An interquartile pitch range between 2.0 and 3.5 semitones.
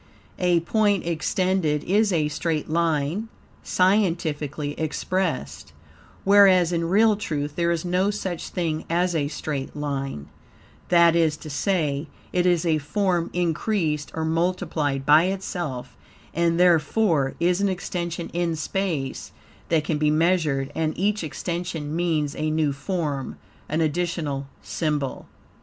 Yes: average, 3.1 semitones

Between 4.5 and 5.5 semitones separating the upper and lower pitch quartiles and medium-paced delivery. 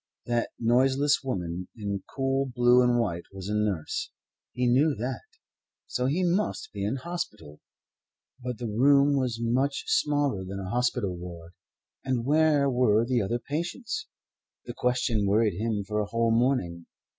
Yes: average, 4.8 semitones; average, 155 wpm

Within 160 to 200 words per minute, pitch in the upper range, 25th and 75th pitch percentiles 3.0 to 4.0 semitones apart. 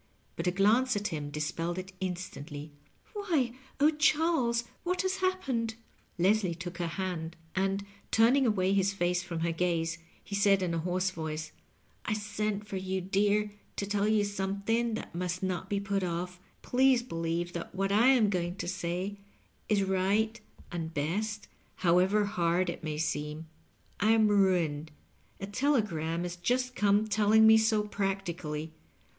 Yes: average, 165 wpm; high, 195 Hz; average, 3.7 semitones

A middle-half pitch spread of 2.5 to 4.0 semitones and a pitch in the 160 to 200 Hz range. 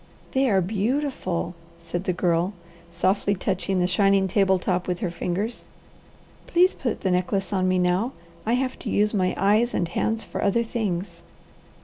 Yes: average, 3.3 semitones; high, 190 Hz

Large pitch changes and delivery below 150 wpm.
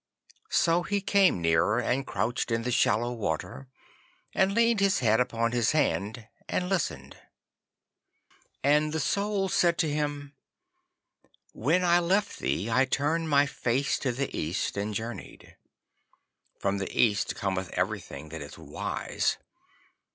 Yes: wide, 8.1 semitones; slow, 135 wpm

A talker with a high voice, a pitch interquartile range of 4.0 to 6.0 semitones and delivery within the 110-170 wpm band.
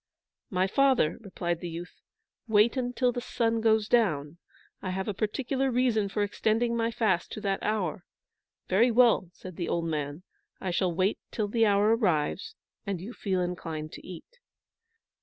Yes: high, 205 Hz; average, 4.5 semitones; average, 165 wpm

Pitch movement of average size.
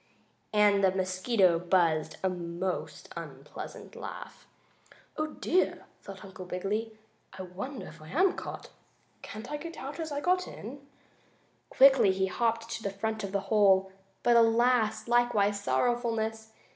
Yes: average, 4.2 semitones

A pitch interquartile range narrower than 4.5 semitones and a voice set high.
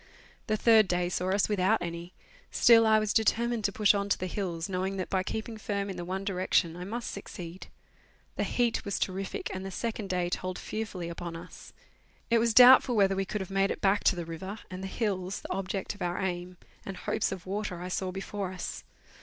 Yes: narrow, 2.5 semitones; high, 195 Hz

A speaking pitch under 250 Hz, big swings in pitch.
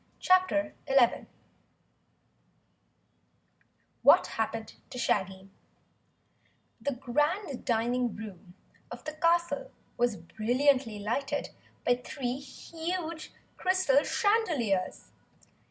No: very high, 260 Hz; wide, 6.0 semitones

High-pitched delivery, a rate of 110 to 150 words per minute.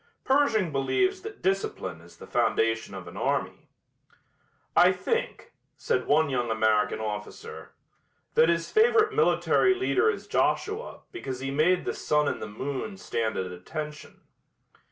No: medium, 155 Hz; average, 140 wpm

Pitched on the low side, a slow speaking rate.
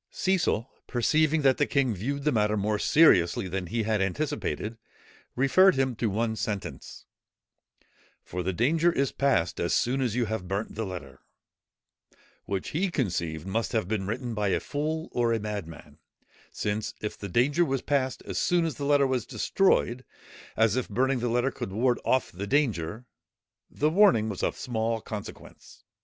No: low, 115 Hz; average, 170 wpm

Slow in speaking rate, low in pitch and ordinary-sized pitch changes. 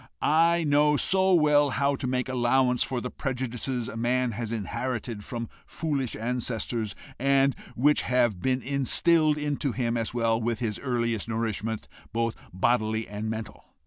No: average, 150 wpm; low, 125 Hz; average, 3.3 semitones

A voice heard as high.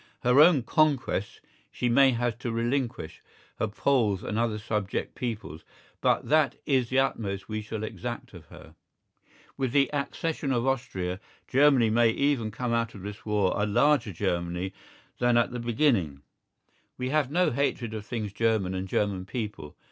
No: low, 115 Hz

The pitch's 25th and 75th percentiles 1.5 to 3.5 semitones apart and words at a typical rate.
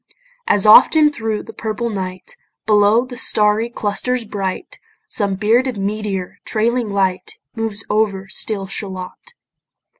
No: narrow, 2.6 semitones; slow, 120 wpm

